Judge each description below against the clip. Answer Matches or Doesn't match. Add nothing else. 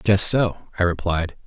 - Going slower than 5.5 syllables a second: Matches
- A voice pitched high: Doesn't match